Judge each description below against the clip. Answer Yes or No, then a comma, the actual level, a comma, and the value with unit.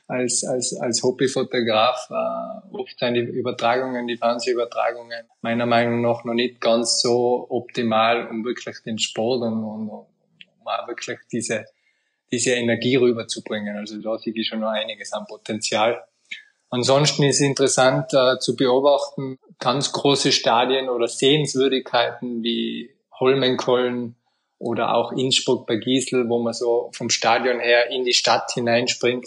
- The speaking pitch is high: No, low, 125 Hz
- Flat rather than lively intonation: Yes, narrow, 1.9 semitones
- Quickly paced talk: No, average, 145 wpm